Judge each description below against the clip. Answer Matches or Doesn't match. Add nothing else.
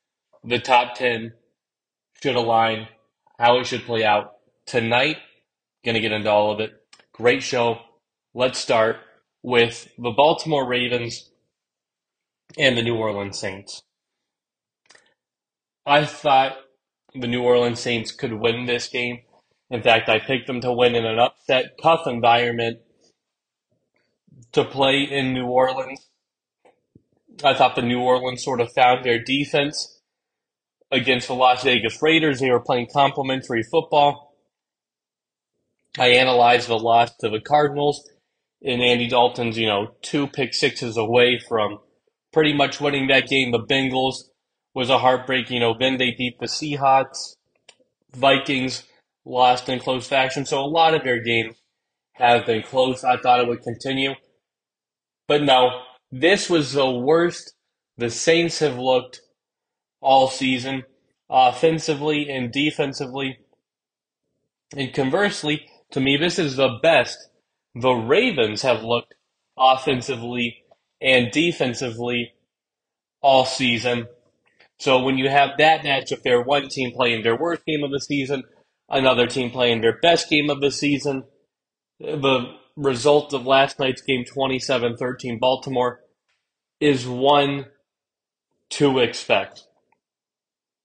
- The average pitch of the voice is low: Matches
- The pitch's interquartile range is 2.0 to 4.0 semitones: Matches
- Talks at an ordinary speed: Doesn't match